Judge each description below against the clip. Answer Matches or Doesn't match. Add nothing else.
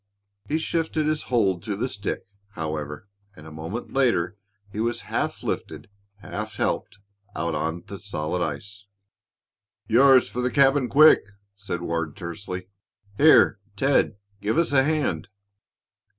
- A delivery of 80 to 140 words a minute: Matches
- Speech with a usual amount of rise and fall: Doesn't match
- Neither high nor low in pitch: Doesn't match